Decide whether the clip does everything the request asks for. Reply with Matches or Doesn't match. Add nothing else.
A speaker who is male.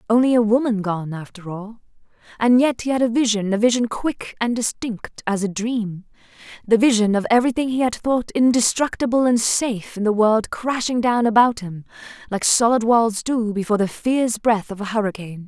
Doesn't match